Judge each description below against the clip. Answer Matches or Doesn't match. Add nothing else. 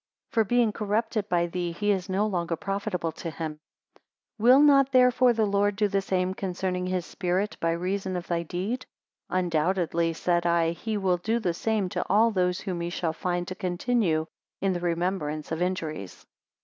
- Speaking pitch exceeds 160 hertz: Matches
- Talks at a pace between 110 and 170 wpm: Doesn't match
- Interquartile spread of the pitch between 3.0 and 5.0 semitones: Matches